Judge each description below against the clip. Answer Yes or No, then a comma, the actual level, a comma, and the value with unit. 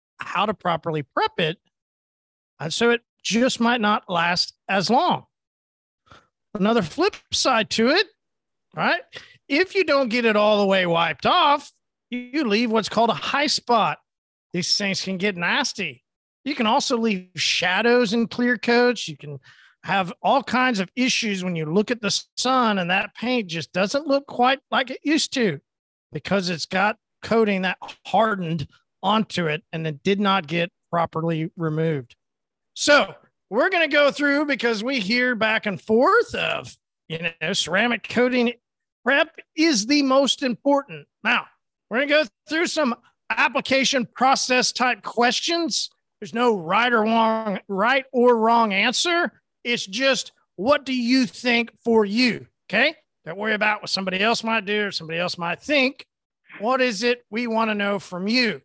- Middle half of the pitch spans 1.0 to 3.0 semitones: No, wide, 5.4 semitones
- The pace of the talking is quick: No, average, 165 wpm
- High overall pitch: Yes, high, 225 Hz